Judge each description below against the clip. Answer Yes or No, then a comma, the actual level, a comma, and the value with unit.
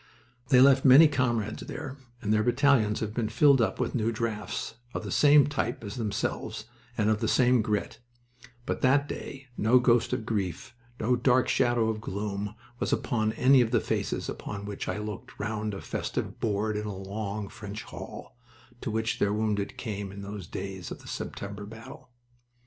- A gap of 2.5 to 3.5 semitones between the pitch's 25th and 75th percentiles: Yes, average, 3.1 semitones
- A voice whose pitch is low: Yes, low, 110 Hz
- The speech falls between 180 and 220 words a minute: Yes, average, 185 wpm